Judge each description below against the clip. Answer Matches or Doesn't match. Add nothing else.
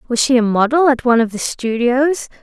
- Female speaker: Matches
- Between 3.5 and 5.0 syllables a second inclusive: Doesn't match